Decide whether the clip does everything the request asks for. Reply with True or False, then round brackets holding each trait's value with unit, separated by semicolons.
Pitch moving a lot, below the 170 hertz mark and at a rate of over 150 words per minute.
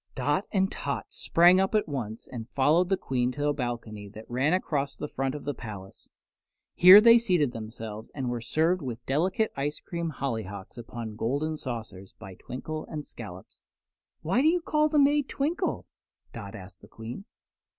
True (7.6 semitones; 140 Hz; 175 wpm)